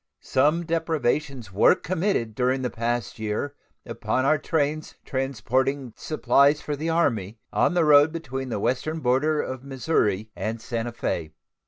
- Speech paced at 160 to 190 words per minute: No, average, 145 wpm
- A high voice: No, low, 135 Hz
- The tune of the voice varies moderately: Yes, average, 4.6 semitones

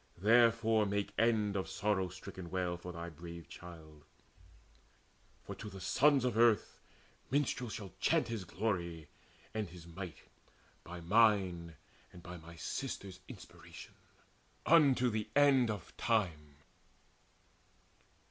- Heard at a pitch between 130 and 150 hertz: No, very low, 95 Hz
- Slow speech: Yes, slow, 120 wpm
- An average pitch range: Yes, average, 4.6 semitones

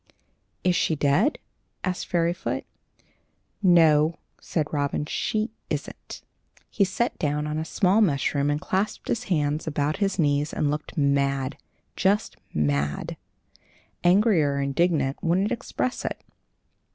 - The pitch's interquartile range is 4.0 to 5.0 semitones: Yes, average, 4.4 semitones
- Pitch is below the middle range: No, medium, 155 Hz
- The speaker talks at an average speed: No, slow, 125 wpm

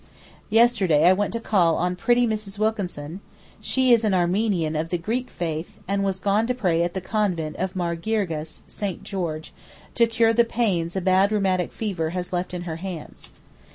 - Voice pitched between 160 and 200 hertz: Yes, high, 190 Hz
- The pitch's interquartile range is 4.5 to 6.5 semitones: No, average, 4.0 semitones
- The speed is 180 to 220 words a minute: Yes, average, 190 wpm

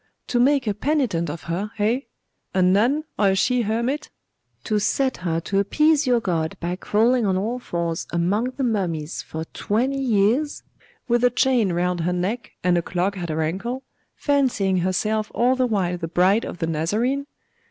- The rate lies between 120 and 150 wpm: No, average, 180 wpm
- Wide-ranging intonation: Yes, wide, 5.7 semitones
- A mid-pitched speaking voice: No, high, 205 Hz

